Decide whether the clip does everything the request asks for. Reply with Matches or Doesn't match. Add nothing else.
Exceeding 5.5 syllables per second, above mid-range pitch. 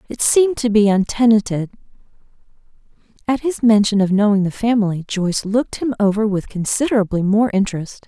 Matches